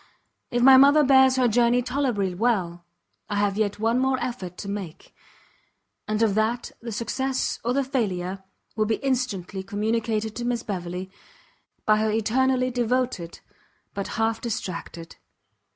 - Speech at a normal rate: Yes, average, 145 wpm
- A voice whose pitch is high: Yes, high, 225 Hz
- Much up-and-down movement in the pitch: No, average, 4.0 semitones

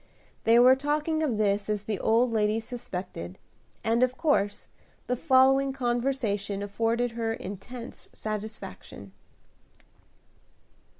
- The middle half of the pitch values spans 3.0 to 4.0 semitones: Yes, average, 3.6 semitones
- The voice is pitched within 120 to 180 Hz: No, high, 230 Hz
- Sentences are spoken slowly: Yes, slow, 110 wpm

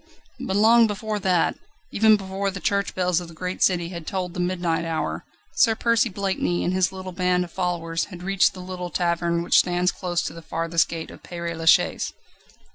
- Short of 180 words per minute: No, average, 200 wpm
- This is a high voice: No, medium, 180 Hz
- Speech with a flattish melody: Yes, narrow, 2.1 semitones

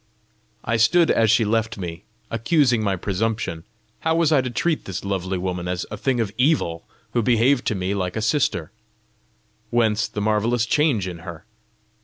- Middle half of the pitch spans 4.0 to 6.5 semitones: Yes, average, 4.4 semitones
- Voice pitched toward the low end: Yes, low, 110 Hz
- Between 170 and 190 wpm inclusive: Yes, average, 175 wpm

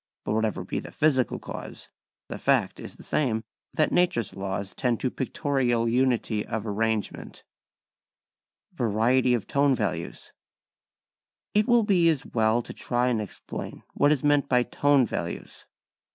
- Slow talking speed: No, average, 150 wpm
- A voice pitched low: Yes, low, 125 Hz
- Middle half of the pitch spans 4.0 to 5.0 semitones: Yes, average, 4.4 semitones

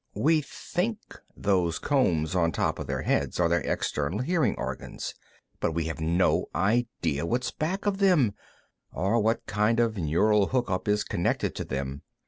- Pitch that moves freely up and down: Yes, wide, 7.1 semitones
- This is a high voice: No, low, 105 Hz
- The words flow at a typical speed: Yes, average, 165 wpm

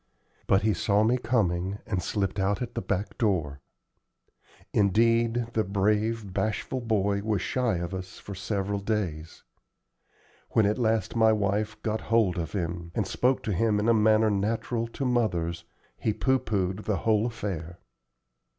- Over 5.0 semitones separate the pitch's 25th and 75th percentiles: No, average, 2.8 semitones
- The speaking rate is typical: Yes, average, 160 wpm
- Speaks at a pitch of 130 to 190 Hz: No, low, 105 Hz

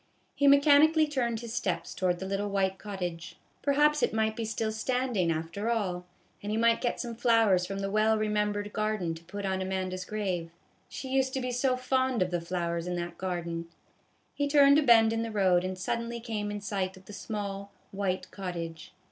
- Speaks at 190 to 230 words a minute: Yes, average, 200 wpm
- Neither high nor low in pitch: No, high, 205 Hz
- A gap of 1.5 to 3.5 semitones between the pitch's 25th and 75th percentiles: No, average, 4.2 semitones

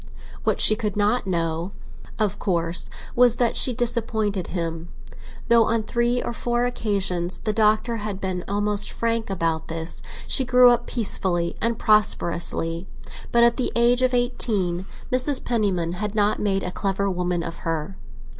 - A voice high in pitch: Yes, high, 205 Hz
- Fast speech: No, average, 155 wpm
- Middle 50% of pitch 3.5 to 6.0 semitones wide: Yes, average, 4.8 semitones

